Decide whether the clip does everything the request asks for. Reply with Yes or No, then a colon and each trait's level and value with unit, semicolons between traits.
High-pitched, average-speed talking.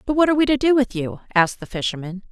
No: high, 235 Hz; fast, 285 wpm